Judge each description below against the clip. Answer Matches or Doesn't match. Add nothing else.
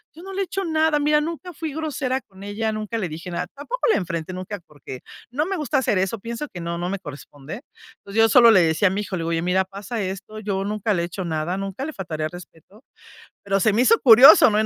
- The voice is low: Doesn't match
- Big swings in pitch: Matches